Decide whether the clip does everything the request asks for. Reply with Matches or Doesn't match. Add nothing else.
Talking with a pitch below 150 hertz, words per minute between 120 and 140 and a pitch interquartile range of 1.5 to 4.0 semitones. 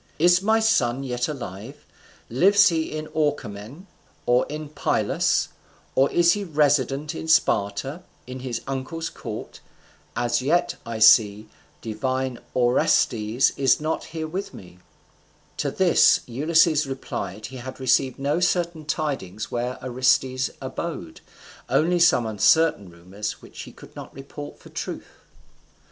Doesn't match